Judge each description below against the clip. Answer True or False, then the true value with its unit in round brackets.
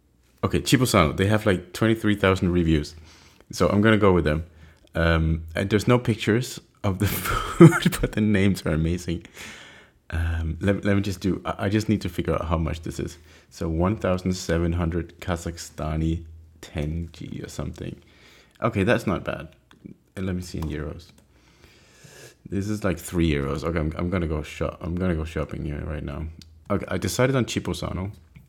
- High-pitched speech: False (85 Hz)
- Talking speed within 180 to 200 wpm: False (170 wpm)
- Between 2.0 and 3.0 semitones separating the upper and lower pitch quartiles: False (3.7 semitones)